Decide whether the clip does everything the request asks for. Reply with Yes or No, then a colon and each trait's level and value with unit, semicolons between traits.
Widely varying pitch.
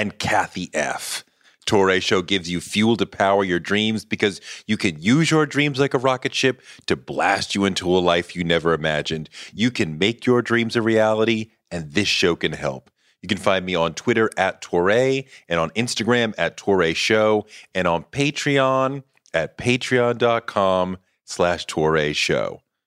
Yes: wide, 5.7 semitones